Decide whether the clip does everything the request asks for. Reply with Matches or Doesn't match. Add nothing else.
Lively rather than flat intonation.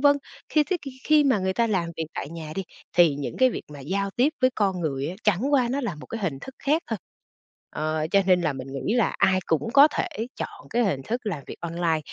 Matches